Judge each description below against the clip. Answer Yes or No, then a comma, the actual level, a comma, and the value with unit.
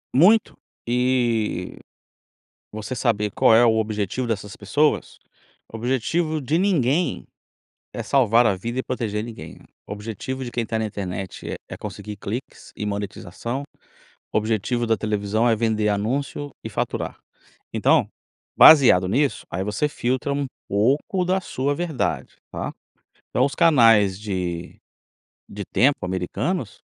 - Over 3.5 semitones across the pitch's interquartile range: Yes, average, 4.5 semitones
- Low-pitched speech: Yes, low, 115 Hz